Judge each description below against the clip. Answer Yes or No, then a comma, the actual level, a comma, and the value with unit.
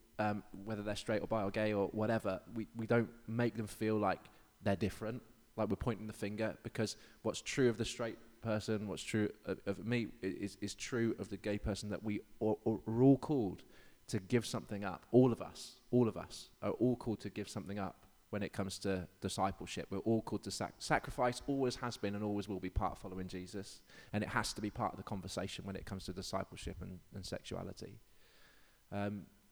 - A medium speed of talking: No, fast, 215 wpm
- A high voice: No, low, 105 Hz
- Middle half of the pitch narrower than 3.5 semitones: Yes, narrow, 2.5 semitones